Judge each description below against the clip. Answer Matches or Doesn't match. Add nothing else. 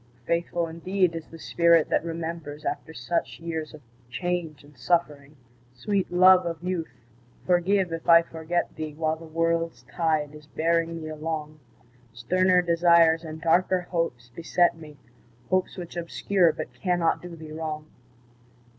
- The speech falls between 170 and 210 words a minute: Doesn't match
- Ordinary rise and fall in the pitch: Doesn't match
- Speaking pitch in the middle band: Matches